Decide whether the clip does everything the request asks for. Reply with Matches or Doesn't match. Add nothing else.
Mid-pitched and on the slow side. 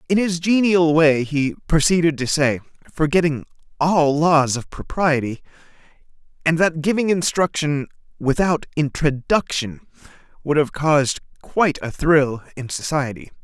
Matches